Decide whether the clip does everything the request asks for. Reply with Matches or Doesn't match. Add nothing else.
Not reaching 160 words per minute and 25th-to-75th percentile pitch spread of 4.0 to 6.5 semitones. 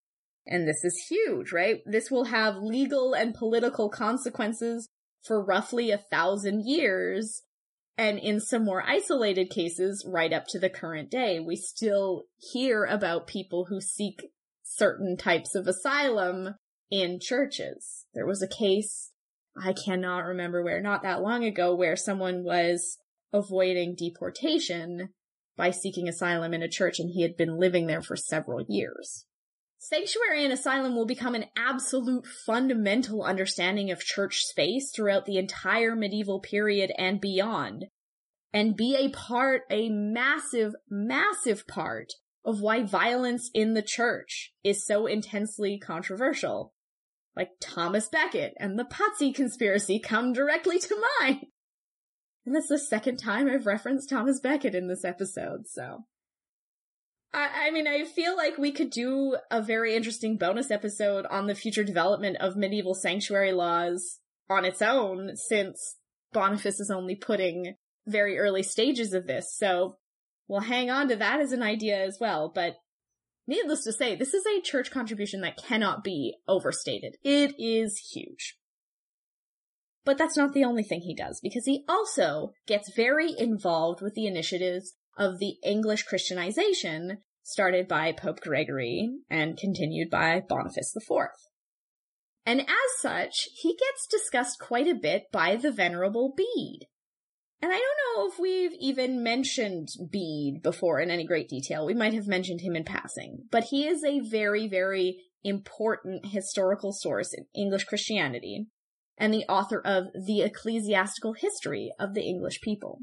Matches